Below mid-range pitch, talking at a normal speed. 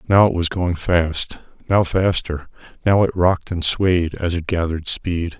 Yes: very low, 85 Hz; average, 180 wpm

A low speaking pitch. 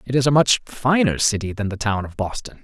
Yes: low, 115 Hz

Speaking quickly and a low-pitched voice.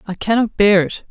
No: fast, 215 wpm; high, 205 Hz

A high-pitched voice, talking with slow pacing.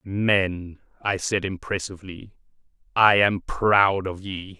No: very low, 95 Hz; slow, 120 wpm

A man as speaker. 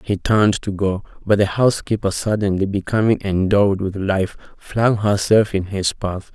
Yes: male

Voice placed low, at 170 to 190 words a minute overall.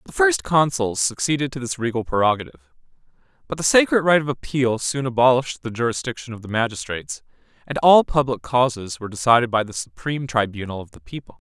Yes: low, 120 Hz; average, 180 wpm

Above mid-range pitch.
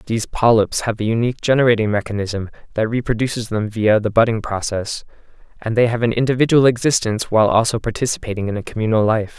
No: low, 110 Hz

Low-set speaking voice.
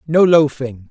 No: medium, 145 Hz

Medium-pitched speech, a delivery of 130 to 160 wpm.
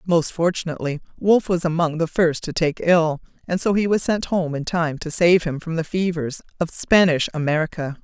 No: medium, 165 Hz; average, 200 wpm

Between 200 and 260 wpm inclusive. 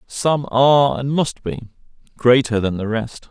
No: average, 165 wpm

